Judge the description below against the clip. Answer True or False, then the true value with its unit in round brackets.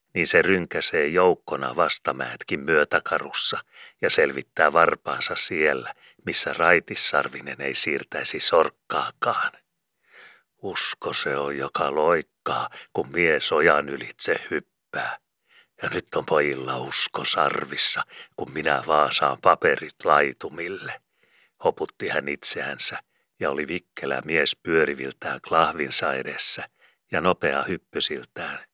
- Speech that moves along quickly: False (100 wpm)